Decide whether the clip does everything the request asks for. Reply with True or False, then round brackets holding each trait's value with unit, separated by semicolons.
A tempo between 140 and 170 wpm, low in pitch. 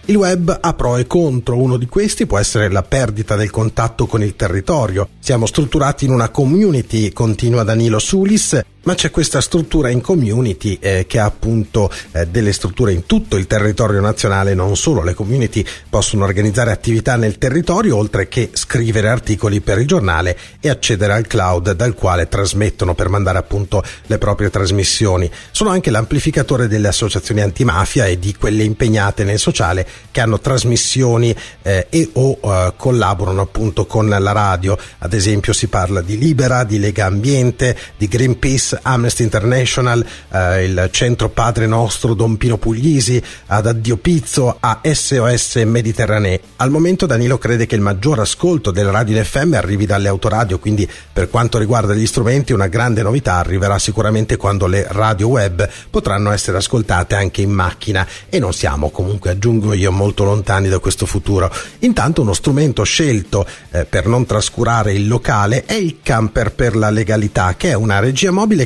True (165 wpm; 110 Hz)